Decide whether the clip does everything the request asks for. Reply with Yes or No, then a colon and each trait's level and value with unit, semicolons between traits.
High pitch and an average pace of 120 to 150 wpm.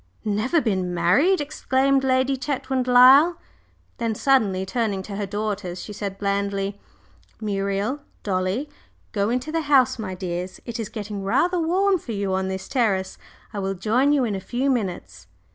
No: high, 215 Hz; average, 160 wpm